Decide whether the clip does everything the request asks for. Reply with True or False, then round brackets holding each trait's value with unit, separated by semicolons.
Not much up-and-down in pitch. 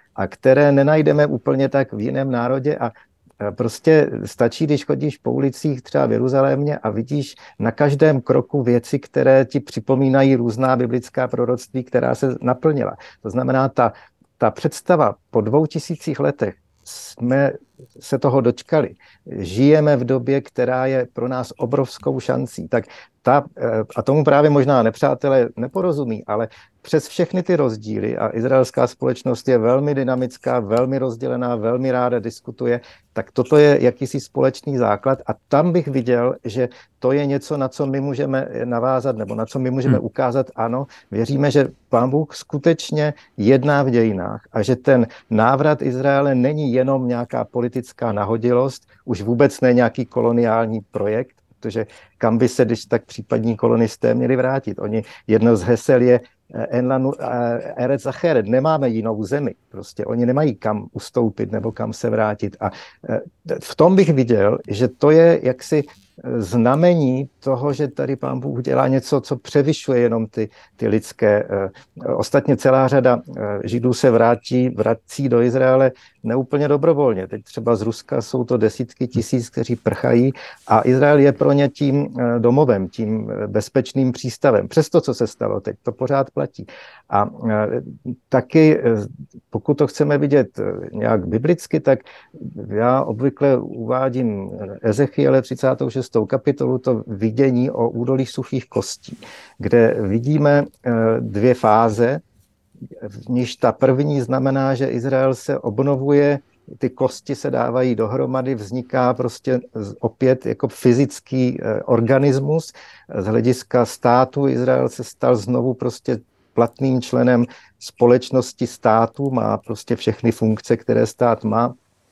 False (3.0 semitones)